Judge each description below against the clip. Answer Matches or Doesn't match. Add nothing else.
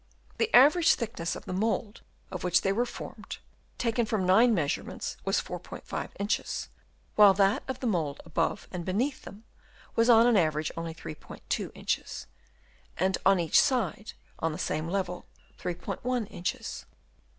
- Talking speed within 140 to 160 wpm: Matches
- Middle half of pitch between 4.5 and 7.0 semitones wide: Matches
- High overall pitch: Matches